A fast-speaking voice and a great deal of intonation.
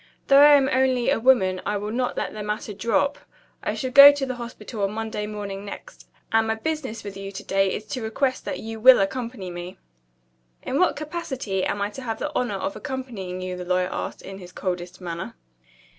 No: fast, 215 wpm; average, 4.9 semitones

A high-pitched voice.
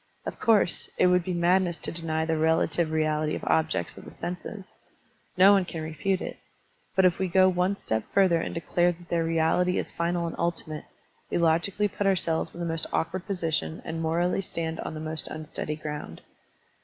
No: medium, 170 Hz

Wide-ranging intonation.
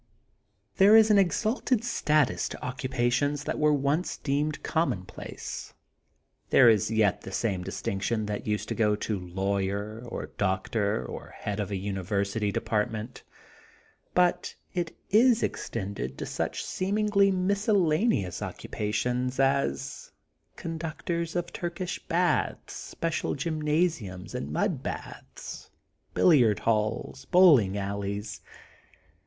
Yes: wide, 8.8 semitones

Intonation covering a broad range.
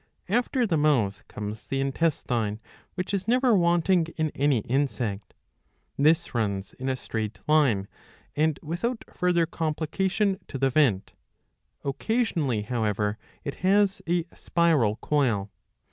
Yes: wide, 7.4 semitones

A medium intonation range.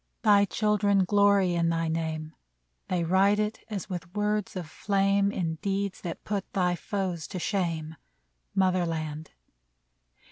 Yes: average, 3.3 semitones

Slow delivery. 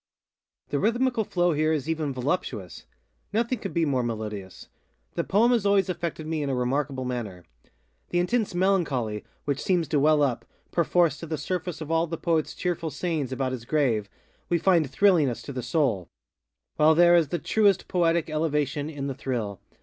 No: average, 175 wpm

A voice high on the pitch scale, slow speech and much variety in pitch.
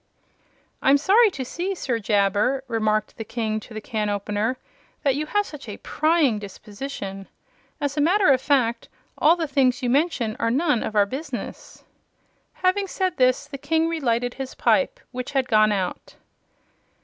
No: very high, 260 Hz; average, 165 wpm; wide, 5.9 semitones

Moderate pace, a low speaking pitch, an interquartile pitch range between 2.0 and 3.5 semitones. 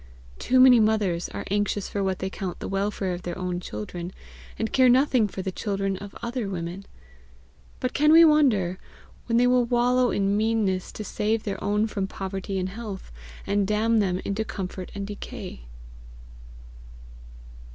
No: average, 165 wpm; high, 205 Hz; average, 3.2 semitones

